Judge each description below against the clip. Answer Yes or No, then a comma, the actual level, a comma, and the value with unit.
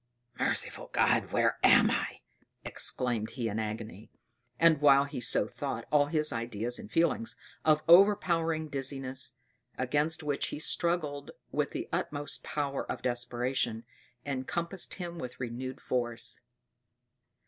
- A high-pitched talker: No, medium, 140 Hz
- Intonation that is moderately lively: Yes, average, 4.4 semitones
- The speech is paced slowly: Yes, slow, 125 wpm